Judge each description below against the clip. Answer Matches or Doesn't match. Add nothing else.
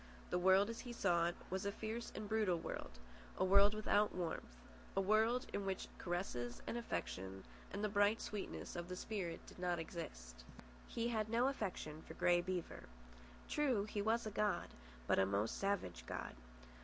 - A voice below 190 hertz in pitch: Doesn't match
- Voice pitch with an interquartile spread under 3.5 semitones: Doesn't match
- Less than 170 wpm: Doesn't match